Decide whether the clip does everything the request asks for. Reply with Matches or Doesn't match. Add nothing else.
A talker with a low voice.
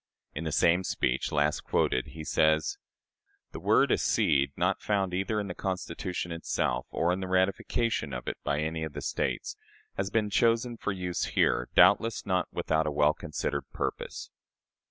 Matches